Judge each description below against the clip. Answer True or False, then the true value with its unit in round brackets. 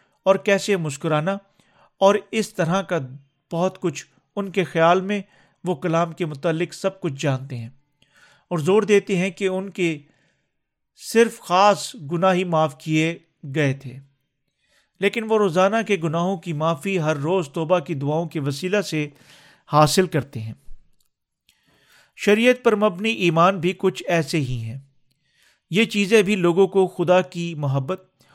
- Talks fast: False (150 wpm)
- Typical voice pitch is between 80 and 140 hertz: False (175 Hz)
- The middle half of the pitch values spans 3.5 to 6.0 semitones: True (4.2 semitones)